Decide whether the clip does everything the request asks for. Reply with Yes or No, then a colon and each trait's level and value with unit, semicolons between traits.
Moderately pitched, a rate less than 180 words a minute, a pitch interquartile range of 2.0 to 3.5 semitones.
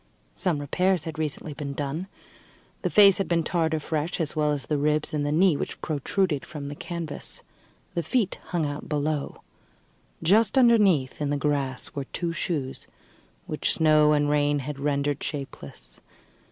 Yes: medium, 150 Hz; average, 165 wpm; average, 2.8 semitones